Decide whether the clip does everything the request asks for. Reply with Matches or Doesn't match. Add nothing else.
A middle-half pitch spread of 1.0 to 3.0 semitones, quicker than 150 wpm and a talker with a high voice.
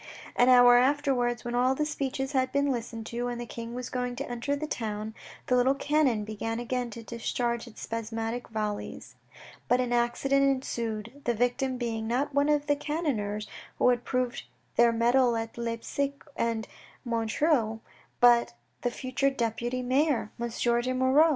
Matches